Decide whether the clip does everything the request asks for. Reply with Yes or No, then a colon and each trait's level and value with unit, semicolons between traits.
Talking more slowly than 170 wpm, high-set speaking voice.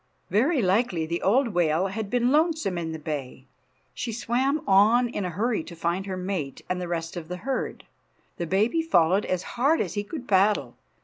No: average, 195 wpm; high, 195 Hz